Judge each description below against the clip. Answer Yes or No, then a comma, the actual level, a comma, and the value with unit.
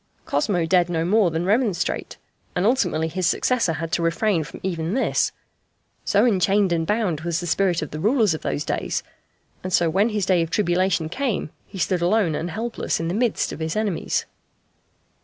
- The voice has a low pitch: No, medium, 180 Hz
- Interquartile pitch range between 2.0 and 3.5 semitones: No, average, 4.0 semitones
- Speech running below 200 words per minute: Yes, average, 190 wpm